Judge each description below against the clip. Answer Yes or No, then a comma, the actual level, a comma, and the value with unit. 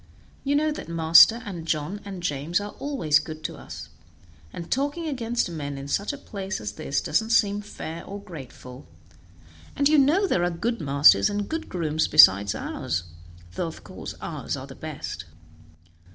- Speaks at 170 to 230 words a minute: Yes, average, 175 wpm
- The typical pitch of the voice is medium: Yes, medium, 180 Hz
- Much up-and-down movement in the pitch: Yes, wide, 7.2 semitones